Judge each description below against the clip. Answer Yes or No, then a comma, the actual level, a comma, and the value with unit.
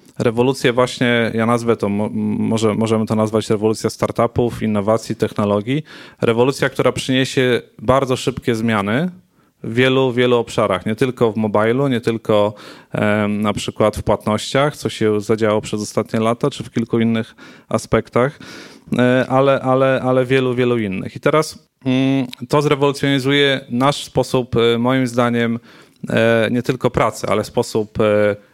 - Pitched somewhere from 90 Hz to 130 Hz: Yes, low, 120 Hz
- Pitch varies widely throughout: No, average, 2.9 semitones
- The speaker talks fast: No, average, 130 wpm